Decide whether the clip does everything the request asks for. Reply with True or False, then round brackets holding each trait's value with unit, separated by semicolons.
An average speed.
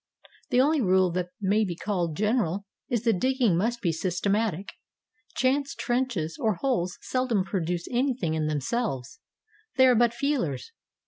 True (150 wpm)